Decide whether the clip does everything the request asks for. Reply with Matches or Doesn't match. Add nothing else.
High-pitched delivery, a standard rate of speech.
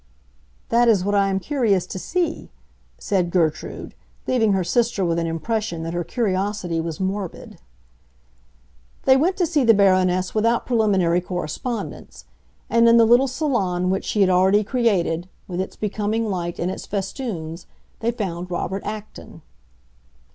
Matches